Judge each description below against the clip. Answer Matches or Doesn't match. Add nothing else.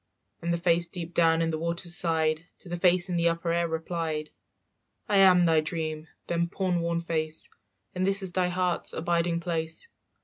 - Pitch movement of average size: Doesn't match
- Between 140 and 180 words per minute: Doesn't match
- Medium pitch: Matches